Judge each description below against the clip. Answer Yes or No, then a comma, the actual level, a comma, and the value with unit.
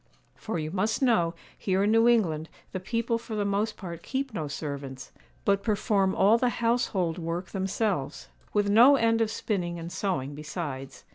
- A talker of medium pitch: No, high, 195 Hz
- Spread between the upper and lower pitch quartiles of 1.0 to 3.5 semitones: No, average, 5.2 semitones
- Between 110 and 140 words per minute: No, average, 170 wpm